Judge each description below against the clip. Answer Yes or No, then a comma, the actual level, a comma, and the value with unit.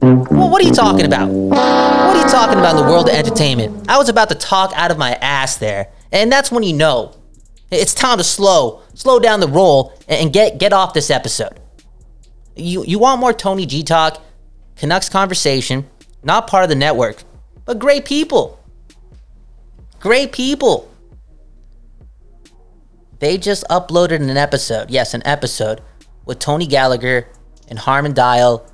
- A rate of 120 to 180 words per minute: Yes, average, 165 wpm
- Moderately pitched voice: Yes, medium, 145 Hz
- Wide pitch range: Yes, wide, 8.7 semitones